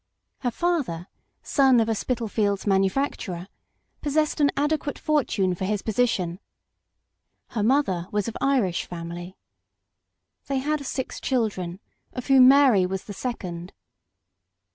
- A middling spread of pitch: No, wide, 6.5 semitones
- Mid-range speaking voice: No, high, 225 Hz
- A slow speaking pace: Yes, slow, 120 wpm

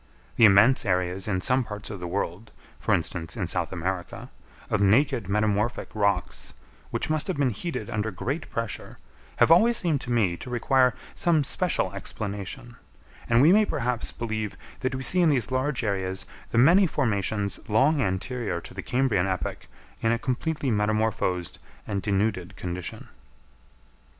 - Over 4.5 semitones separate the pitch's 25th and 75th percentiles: Yes, average, 4.9 semitones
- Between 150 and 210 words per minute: Yes, average, 160 wpm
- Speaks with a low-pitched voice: Yes, low, 110 Hz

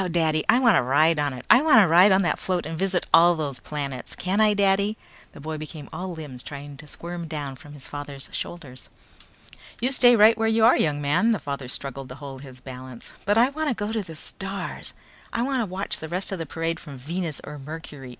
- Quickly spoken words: Yes, fast, 220 wpm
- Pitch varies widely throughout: Yes, wide, 5.7 semitones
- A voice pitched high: No, medium, 165 Hz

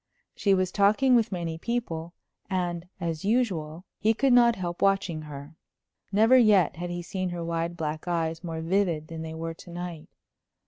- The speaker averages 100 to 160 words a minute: No, average, 175 wpm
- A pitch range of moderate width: Yes, average, 3.5 semitones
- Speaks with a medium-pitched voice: Yes, medium, 175 Hz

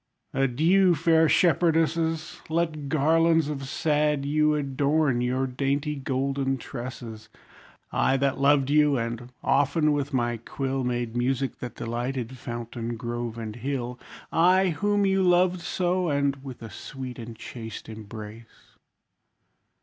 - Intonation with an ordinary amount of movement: Yes, average, 4.3 semitones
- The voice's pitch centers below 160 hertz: Yes, low, 135 Hz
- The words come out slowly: Yes, slow, 125 wpm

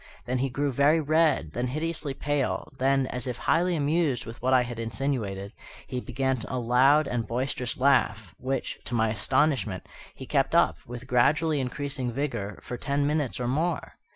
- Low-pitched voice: Yes, low, 130 Hz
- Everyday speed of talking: Yes, average, 175 wpm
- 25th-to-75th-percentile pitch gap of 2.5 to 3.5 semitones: Yes, average, 3.0 semitones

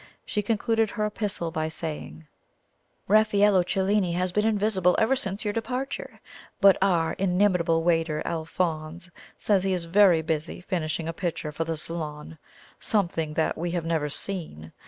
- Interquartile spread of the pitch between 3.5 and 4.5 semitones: Yes, average, 4.1 semitones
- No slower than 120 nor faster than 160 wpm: Yes, average, 150 wpm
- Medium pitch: Yes, medium, 175 Hz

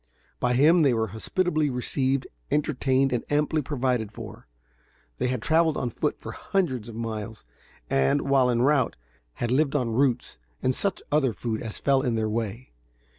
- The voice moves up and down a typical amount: Yes, average, 4.0 semitones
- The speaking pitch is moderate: No, low, 130 Hz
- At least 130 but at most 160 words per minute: No, average, 170 wpm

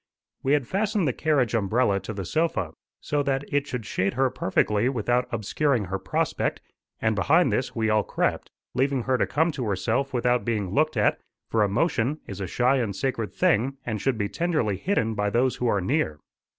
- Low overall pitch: Yes, low, 120 Hz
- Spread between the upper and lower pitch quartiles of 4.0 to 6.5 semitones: Yes, average, 4.9 semitones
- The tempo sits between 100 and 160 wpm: No, average, 195 wpm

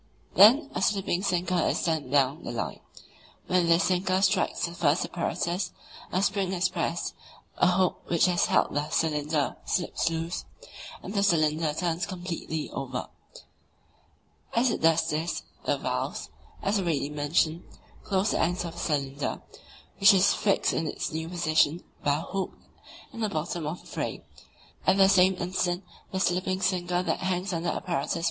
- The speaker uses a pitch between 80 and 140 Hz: No, medium, 175 Hz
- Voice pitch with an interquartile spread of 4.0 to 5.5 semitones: No, average, 2.8 semitones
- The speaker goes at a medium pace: Yes, average, 170 wpm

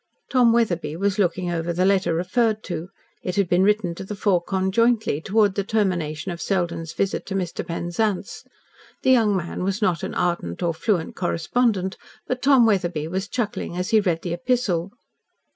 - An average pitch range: Yes, average, 3.6 semitones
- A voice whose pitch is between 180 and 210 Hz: Yes, high, 190 Hz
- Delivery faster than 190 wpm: No, average, 175 wpm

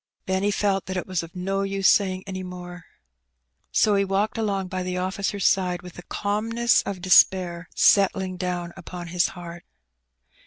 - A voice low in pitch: No, medium, 185 Hz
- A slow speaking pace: No, average, 165 wpm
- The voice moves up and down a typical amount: No, narrow, 1.6 semitones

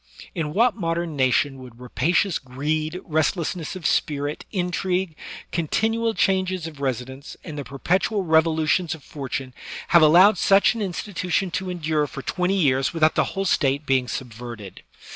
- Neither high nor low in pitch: Yes, medium, 160 Hz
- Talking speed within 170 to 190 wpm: No, average, 150 wpm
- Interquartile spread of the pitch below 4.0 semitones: No, average, 4.9 semitones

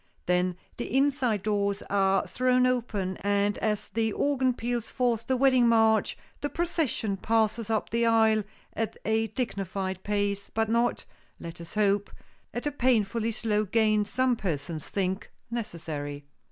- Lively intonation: No, average, 3.1 semitones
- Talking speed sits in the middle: Yes, average, 145 wpm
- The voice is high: Yes, high, 220 Hz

